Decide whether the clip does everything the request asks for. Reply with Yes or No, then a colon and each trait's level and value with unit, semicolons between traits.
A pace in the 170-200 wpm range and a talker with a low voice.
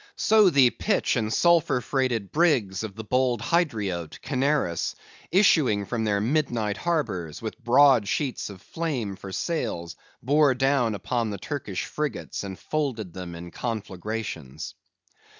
No: slow, 135 wpm; low, 120 Hz